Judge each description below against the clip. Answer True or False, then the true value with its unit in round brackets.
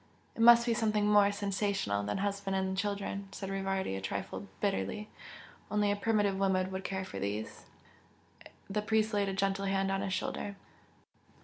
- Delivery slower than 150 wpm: False (170 wpm)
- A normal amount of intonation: False (1.4 semitones)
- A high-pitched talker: True (195 Hz)